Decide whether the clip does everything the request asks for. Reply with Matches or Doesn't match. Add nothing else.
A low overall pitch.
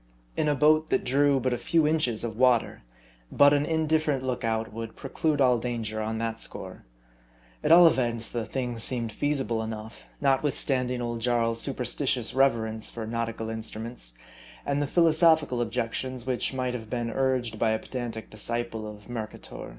Matches